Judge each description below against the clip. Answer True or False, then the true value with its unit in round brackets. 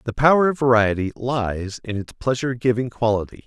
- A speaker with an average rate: True (175 wpm)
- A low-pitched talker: True (120 Hz)